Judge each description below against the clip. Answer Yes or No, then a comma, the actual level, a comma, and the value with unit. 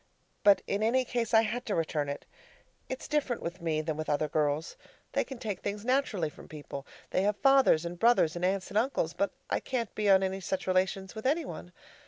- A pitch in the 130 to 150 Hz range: No, high, 195 Hz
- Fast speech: Yes, fast, 220 wpm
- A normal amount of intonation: No, wide, 5.9 semitones